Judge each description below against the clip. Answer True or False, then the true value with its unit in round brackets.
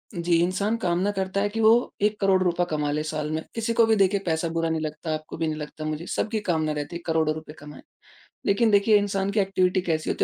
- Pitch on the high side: False (175 Hz)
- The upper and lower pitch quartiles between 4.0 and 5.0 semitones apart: True (4.3 semitones)